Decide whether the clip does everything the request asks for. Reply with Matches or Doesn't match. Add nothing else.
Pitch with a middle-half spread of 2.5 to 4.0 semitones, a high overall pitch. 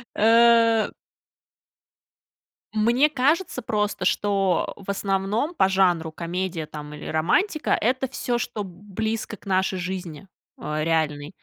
Doesn't match